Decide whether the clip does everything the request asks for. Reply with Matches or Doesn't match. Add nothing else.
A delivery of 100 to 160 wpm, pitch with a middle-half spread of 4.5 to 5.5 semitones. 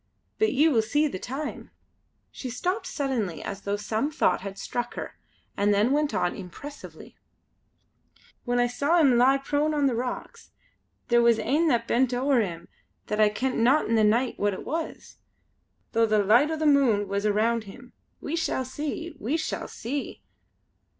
Doesn't match